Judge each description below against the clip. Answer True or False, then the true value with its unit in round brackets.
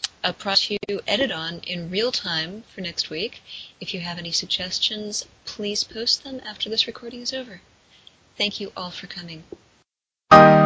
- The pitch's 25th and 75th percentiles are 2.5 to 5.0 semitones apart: True (4.1 semitones)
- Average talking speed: True (165 wpm)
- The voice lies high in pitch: True (200 Hz)